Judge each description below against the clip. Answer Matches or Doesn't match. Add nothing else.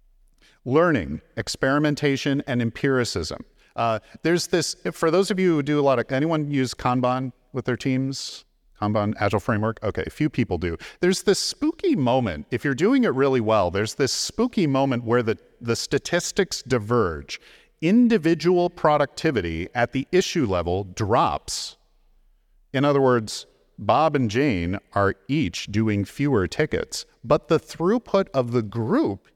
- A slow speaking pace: Doesn't match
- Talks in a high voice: Doesn't match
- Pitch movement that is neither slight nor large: Doesn't match